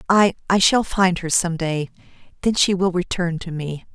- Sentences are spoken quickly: No, average, 180 wpm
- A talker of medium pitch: Yes, medium, 180 Hz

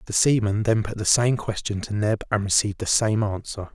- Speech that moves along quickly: Yes, fast, 225 wpm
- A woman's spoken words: No, male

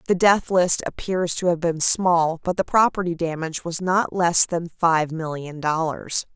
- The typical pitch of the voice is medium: Yes, medium, 170 Hz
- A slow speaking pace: No, average, 180 wpm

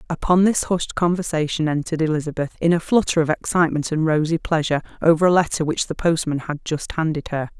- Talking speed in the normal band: Yes, average, 190 wpm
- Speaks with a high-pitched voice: No, medium, 160 Hz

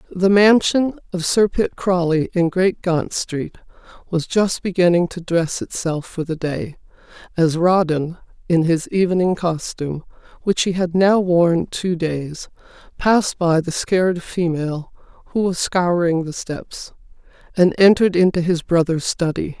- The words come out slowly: No, average, 145 wpm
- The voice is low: No, medium, 175 Hz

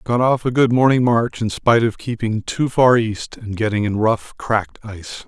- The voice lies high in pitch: No, low, 115 Hz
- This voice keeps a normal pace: No, fast, 215 wpm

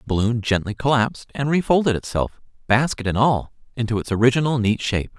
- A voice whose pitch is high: No, low, 120 Hz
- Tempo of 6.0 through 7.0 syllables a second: Yes, 6.3 syllables/s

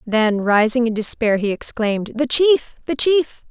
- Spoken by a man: No, female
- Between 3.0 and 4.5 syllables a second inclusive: Yes, 4.4 syllables/s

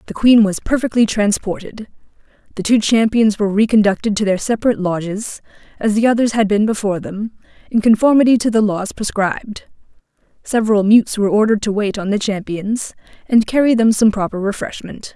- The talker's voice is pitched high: Yes, high, 215 Hz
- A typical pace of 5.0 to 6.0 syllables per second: Yes, 5.8 syllables/s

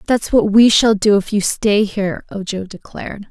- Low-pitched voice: No, high, 205 Hz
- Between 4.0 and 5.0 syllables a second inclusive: Yes, 4.9 syllables/s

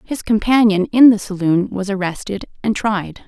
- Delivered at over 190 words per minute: No, average, 165 wpm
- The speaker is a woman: Yes, female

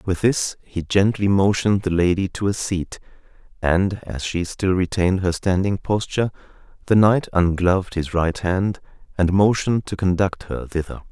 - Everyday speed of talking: Yes, average, 160 wpm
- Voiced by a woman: No, male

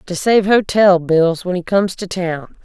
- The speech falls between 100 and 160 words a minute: No, fast, 205 wpm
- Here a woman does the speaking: Yes, female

